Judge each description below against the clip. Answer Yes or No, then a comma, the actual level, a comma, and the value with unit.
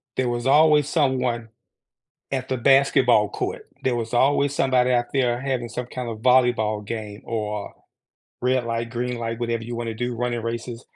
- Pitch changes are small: Yes, narrow, 1.9 semitones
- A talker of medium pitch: No, low, 120 Hz